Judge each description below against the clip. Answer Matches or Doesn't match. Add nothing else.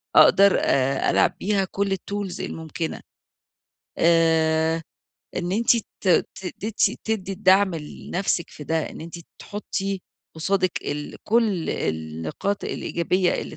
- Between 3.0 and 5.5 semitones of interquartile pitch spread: Matches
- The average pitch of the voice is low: Doesn't match